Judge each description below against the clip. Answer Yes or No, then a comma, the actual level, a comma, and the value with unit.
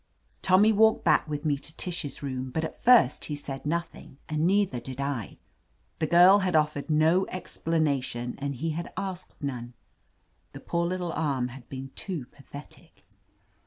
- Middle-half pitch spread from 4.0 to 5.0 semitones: Yes, average, 4.3 semitones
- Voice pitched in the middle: Yes, medium, 155 Hz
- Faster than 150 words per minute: Yes, average, 165 wpm